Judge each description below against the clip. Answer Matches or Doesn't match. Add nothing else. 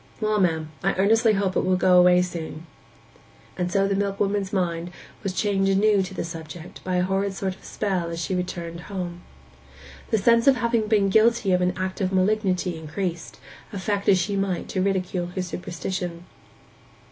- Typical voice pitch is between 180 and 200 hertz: Matches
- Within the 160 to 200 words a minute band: Matches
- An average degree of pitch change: Doesn't match